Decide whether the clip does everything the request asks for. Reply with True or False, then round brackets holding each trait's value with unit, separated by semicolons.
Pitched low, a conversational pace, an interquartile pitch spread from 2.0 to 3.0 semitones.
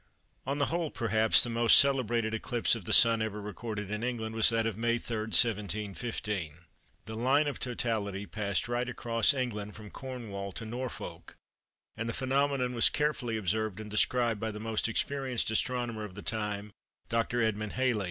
True (115 Hz; 170 wpm; 2.5 semitones)